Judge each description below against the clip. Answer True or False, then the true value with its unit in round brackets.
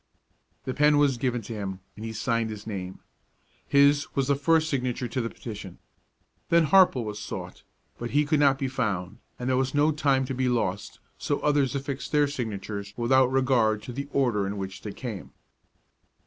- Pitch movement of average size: True (4.5 semitones)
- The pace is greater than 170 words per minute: True (190 wpm)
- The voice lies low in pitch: True (125 Hz)